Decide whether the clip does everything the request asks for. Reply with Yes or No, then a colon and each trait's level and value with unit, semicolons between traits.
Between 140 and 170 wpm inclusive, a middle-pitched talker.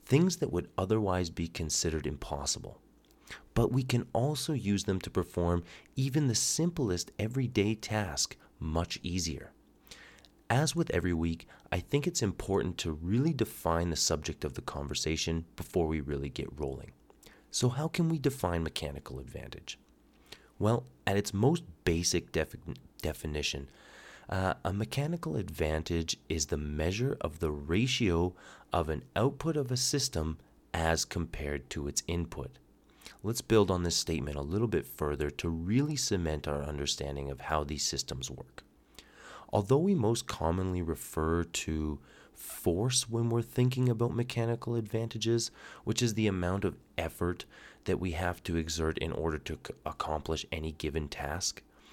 No: average, 150 wpm; very low, 90 Hz